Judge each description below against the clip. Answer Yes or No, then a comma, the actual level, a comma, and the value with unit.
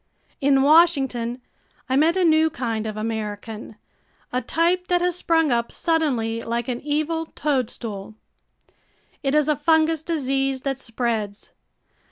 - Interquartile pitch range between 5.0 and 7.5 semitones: Yes, wide, 5.5 semitones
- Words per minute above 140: No, slow, 135 wpm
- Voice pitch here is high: Yes, very high, 270 Hz